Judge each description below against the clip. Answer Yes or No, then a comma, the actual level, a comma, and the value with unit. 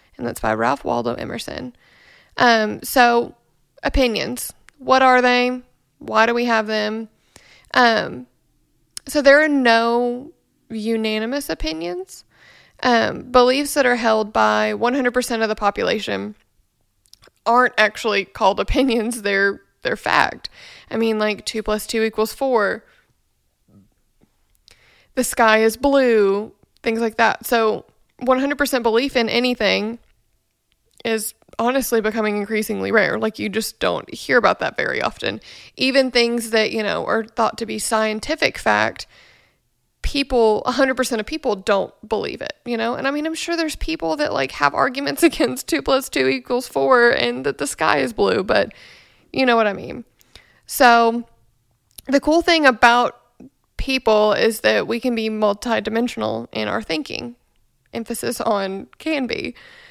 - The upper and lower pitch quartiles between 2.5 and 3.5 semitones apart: Yes, average, 3.1 semitones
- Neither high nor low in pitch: No, high, 230 Hz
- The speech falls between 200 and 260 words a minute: No, average, 145 wpm